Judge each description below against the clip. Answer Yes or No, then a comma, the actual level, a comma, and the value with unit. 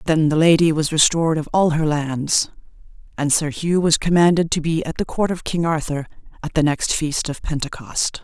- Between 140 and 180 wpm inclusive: No, fast, 205 wpm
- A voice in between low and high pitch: Yes, medium, 160 Hz